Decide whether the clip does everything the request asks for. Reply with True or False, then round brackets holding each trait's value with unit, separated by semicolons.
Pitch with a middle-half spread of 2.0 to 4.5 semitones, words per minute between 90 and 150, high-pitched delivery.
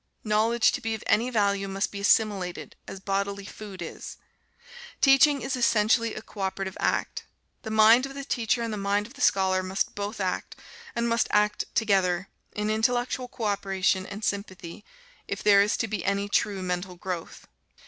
False (2.6 semitones; 180 wpm; 205 Hz)